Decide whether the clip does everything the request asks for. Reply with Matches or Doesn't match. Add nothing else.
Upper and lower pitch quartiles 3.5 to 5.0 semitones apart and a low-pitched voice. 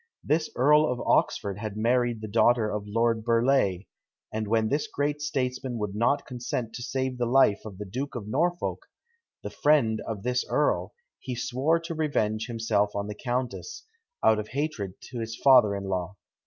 Matches